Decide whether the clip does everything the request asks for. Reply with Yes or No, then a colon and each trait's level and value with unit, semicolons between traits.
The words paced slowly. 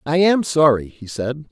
No: average, 200 wpm